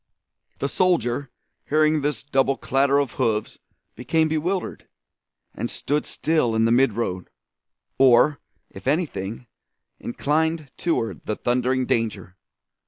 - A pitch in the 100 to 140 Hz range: Yes, low, 135 Hz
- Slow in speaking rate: Yes, slow, 110 wpm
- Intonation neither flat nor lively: Yes, average, 4.5 semitones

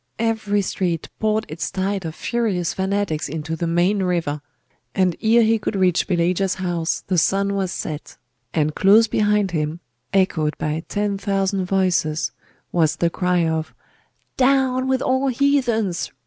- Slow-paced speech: No, average, 150 wpm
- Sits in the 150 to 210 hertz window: Yes, high, 190 Hz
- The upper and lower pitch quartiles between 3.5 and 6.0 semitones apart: Yes, average, 3.9 semitones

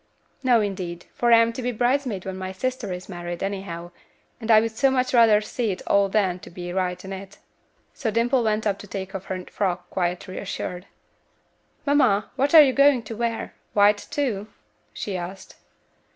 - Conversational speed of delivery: Yes, average, 190 wpm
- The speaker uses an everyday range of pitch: Yes, average, 4.2 semitones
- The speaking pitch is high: Yes, high, 205 Hz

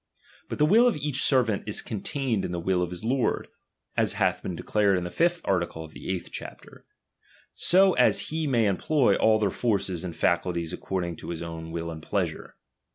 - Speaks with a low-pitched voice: Yes, low, 100 Hz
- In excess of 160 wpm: Yes, fast, 205 wpm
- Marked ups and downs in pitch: Yes, wide, 7.5 semitones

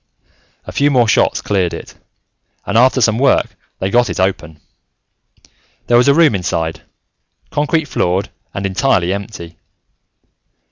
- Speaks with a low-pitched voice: Yes, low, 105 Hz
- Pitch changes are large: Yes, wide, 6.1 semitones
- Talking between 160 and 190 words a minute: No, slow, 135 wpm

